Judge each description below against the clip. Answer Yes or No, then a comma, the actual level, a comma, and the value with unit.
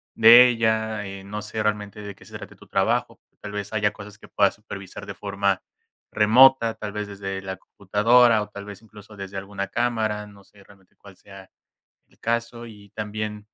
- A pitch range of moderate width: No, narrow, 1.7 semitones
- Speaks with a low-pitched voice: Yes, low, 105 Hz